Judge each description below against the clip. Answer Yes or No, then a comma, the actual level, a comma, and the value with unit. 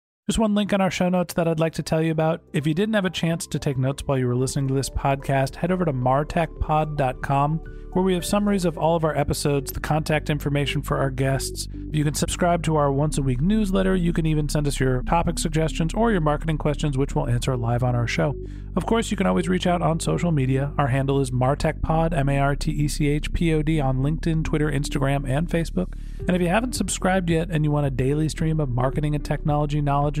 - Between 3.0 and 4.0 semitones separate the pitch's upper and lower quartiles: Yes, average, 3.5 semitones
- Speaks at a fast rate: Yes, fast, 245 wpm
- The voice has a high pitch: No, medium, 150 Hz